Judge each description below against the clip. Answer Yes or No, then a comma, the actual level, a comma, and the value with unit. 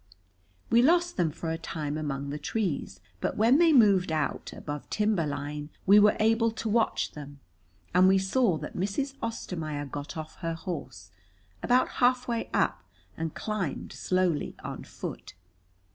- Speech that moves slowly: No, average, 155 wpm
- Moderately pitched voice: Yes, medium, 180 Hz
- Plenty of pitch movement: Yes, wide, 7.0 semitones